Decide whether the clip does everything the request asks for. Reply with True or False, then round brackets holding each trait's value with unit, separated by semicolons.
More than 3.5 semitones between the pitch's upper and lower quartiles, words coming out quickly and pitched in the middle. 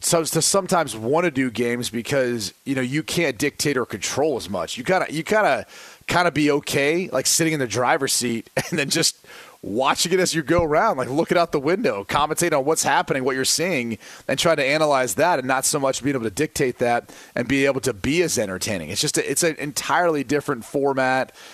True (4.1 semitones; 240 wpm; 145 Hz)